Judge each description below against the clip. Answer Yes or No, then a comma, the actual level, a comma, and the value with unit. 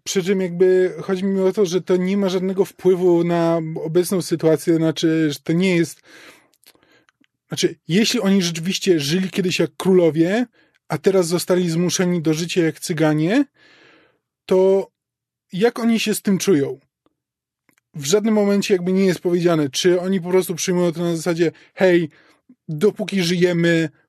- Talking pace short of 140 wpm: No, average, 155 wpm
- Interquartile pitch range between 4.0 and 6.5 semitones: No, narrow, 2.4 semitones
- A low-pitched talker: No, medium, 180 Hz